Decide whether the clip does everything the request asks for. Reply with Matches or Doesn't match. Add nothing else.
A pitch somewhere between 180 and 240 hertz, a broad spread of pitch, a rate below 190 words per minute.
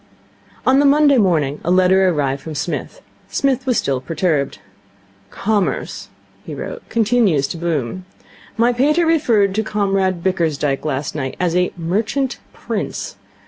Matches